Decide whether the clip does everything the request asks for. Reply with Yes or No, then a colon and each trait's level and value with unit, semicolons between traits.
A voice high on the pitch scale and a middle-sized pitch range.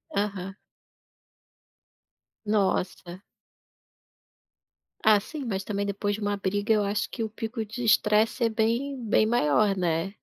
No: high, 210 Hz; narrow, 2.0 semitones